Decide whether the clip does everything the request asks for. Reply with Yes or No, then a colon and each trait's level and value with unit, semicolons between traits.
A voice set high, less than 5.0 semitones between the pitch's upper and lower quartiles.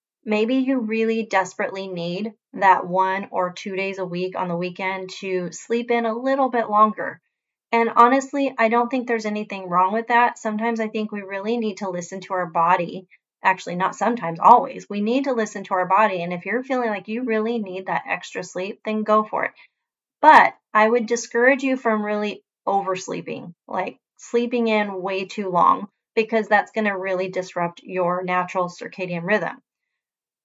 Yes: high, 210 Hz; average, 3.7 semitones